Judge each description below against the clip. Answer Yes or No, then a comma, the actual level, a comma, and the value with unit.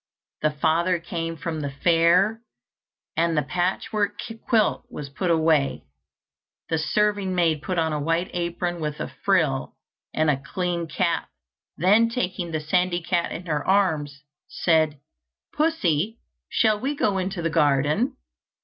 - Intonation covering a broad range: No, average, 3.3 semitones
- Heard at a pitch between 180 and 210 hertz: No, medium, 170 Hz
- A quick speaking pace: No, average, 140 wpm